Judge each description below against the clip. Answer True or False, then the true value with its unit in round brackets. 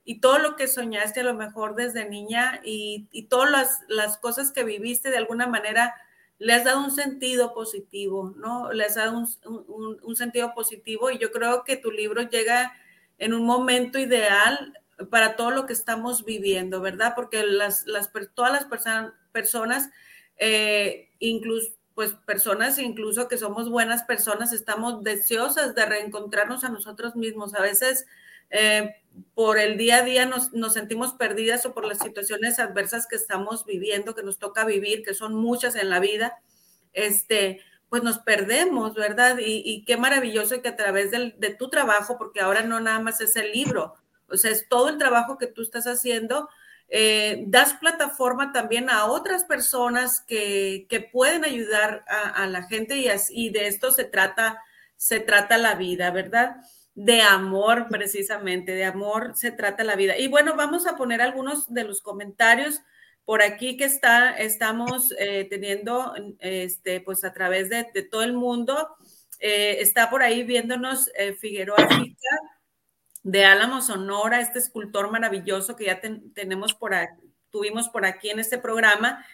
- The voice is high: True (225 Hz)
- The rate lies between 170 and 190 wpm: True (175 wpm)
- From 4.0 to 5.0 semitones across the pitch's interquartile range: False (2.8 semitones)